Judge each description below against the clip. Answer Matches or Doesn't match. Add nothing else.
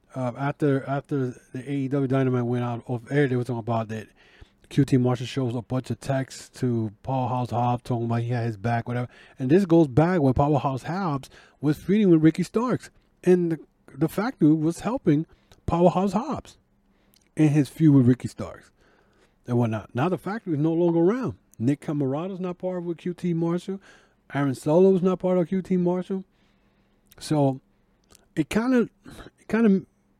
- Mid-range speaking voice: Matches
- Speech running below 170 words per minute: Doesn't match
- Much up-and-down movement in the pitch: Matches